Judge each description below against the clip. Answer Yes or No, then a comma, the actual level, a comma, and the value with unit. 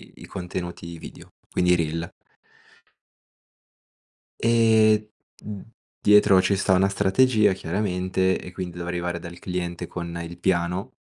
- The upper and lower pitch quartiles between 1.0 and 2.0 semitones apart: No, narrow, 2.6 semitones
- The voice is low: Yes, very low, 90 Hz